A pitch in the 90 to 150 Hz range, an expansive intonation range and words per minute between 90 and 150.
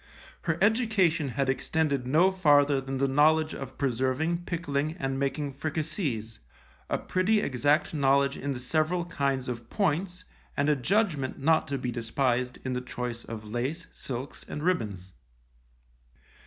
No: medium, 140 Hz; average, 4.0 semitones; average, 145 wpm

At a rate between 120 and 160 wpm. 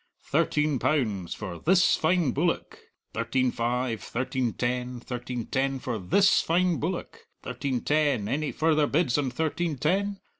Yes: average, 140 wpm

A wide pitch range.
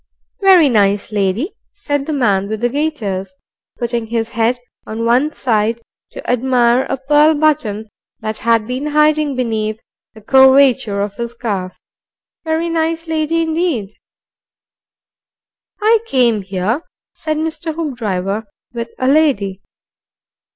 Yes: wide, 5.9 semitones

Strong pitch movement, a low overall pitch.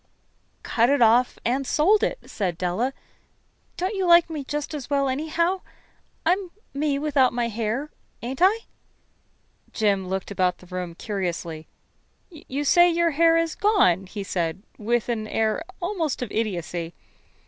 No: wide, 8.5 semitones; very high, 255 Hz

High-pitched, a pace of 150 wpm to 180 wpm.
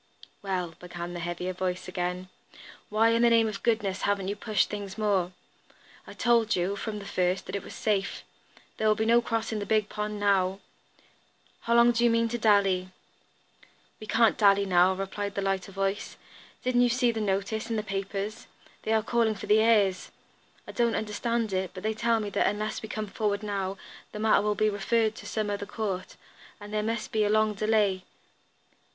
No: high, 210 Hz; average, 200 wpm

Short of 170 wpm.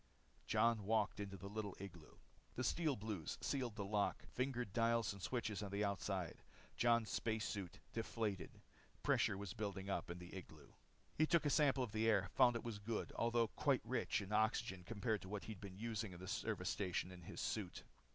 No: average, 200 wpm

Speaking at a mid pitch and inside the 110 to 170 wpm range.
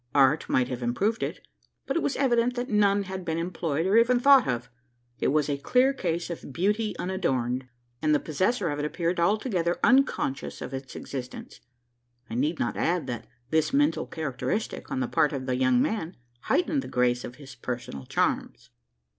No: medium, 165 Hz; average, 185 wpm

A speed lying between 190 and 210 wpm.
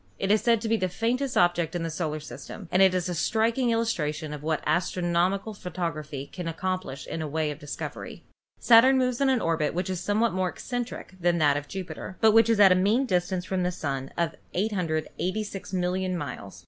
Yes: fast, 205 wpm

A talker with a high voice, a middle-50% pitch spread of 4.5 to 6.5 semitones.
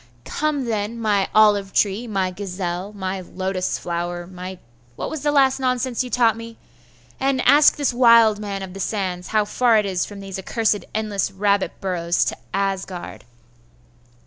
No: high, 205 Hz; average, 3.5 semitones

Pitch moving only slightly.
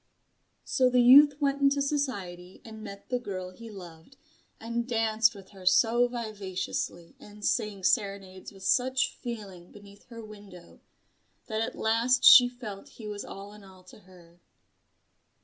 No: average, 4.2 semitones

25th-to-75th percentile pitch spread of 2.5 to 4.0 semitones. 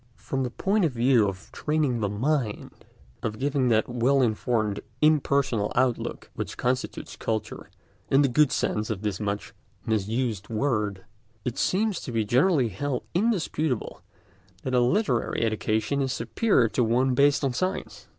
No: average, 4.4 semitones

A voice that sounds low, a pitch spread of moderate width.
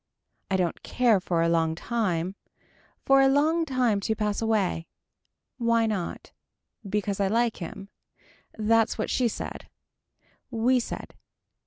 No: high, 220 Hz; average, 3.9 semitones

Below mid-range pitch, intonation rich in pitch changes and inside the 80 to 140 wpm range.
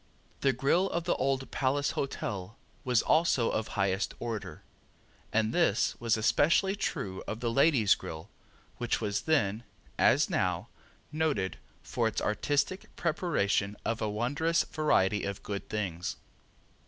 Yes: low, 115 Hz; wide, 6.3 semitones; slow, 135 wpm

